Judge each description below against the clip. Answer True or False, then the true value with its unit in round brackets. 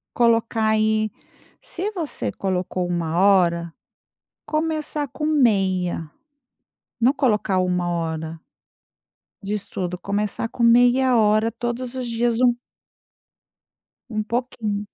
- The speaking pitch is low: False (215 Hz)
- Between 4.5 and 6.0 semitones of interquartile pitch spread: True (4.9 semitones)